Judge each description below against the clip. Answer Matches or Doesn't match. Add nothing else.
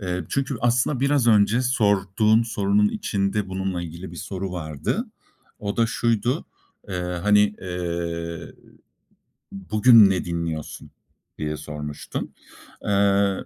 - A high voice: Doesn't match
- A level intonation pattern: Doesn't match